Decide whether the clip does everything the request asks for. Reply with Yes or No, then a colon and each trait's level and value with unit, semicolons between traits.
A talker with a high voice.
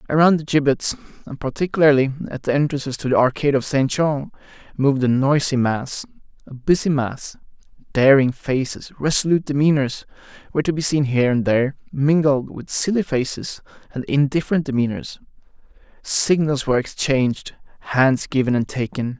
No: medium, 140 Hz